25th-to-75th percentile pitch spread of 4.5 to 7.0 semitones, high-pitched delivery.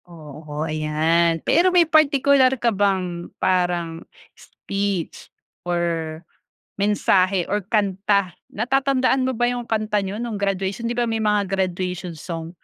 Yes: average, 5.2 semitones; high, 195 Hz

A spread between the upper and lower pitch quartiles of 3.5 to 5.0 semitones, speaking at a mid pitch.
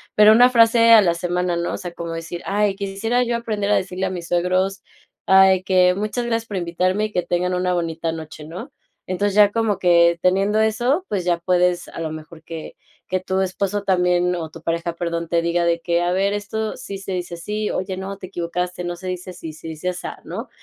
No: average, 2.9 semitones; medium, 180 Hz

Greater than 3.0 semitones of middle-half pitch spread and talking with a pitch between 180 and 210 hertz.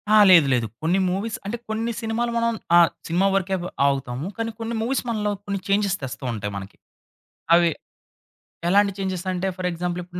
Yes: average, 4.2 semitones; high, 190 Hz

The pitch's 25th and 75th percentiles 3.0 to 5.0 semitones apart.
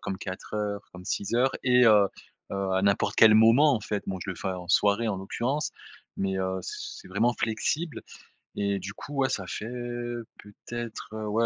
Yes: average, 3.4 semitones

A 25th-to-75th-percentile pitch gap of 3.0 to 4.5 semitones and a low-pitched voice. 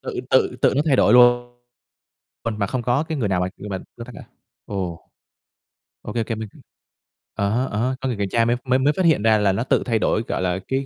Yes: average, 4.0 semitones; low, 115 Hz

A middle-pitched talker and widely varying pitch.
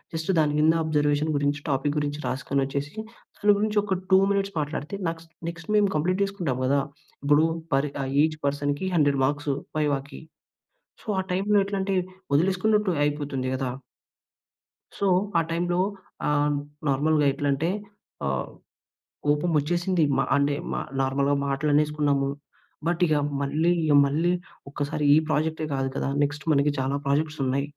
No: medium, 150 Hz; average, 3.1 semitones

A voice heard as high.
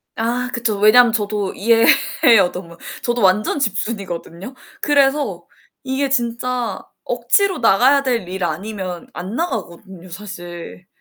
Yes: high, 215 Hz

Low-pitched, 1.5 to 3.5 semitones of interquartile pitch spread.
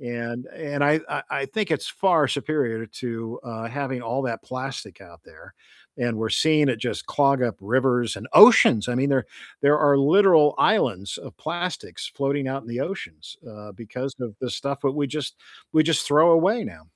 No: low, 130 Hz; average, 4.2 semitones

